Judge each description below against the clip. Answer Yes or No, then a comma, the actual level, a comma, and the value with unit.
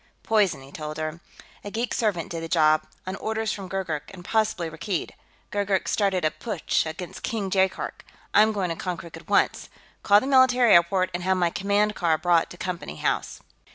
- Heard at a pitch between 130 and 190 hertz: Yes, medium, 185 Hz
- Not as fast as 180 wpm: No, average, 190 wpm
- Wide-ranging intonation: No, average, 3.7 semitones